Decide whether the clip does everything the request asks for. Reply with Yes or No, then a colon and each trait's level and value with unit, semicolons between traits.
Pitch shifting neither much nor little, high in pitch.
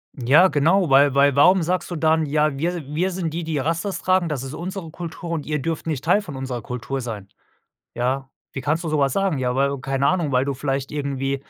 No: average, 3.7 semitones; medium, 150 Hz